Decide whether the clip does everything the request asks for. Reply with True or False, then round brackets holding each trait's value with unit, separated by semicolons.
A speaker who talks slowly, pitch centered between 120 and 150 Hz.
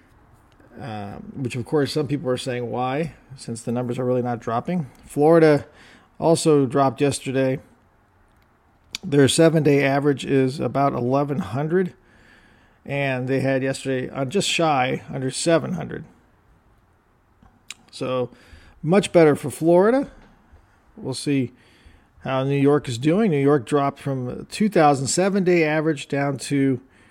True (130 wpm; 135 Hz)